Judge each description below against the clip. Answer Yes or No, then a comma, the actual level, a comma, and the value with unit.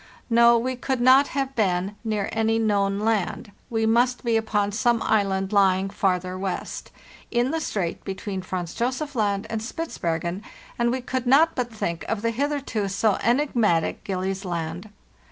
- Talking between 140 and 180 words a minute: Yes, average, 160 wpm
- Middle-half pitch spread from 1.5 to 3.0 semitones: No, average, 3.9 semitones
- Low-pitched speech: No, high, 215 Hz